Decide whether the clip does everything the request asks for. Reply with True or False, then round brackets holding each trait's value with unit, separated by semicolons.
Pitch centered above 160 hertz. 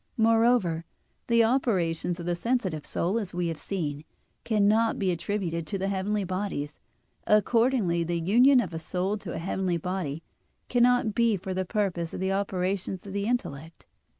True (190 Hz)